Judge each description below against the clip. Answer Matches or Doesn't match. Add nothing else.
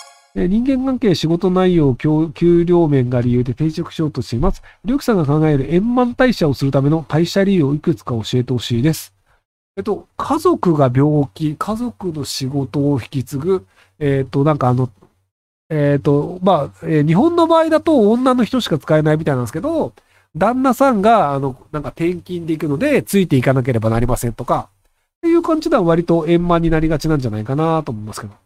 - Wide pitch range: Matches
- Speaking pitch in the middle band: Matches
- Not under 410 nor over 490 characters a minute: Doesn't match